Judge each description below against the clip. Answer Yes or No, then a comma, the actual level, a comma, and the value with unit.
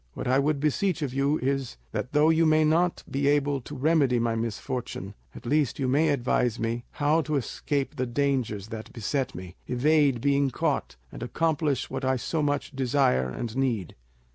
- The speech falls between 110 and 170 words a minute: No, average, 185 wpm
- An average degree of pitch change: Yes, average, 3.5 semitones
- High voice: No, low, 135 Hz